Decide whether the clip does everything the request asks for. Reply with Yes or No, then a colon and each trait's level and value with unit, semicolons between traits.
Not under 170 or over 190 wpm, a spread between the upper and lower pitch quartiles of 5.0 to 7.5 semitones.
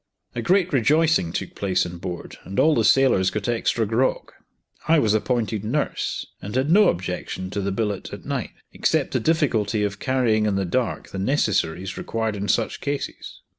Yes: average, 180 wpm; average, 5.3 semitones